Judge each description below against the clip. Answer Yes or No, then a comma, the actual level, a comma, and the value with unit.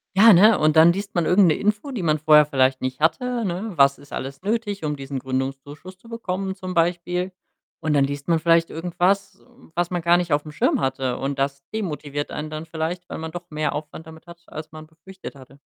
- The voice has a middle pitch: Yes, medium, 160 Hz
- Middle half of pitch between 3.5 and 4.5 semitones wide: Yes, average, 4.0 semitones